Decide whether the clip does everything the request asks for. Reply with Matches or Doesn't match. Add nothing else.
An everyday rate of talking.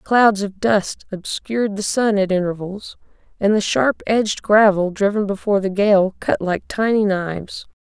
Matches